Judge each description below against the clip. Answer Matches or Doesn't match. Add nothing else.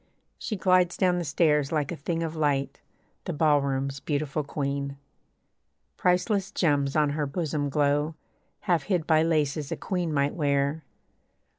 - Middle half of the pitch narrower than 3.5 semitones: Matches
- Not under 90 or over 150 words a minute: Matches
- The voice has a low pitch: Doesn't match